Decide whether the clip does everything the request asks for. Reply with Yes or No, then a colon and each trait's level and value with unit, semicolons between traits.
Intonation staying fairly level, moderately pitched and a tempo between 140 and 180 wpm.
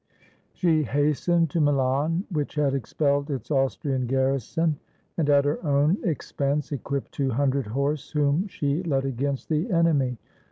Yes: narrow, 2.3 semitones; medium, 145 Hz; average, 145 wpm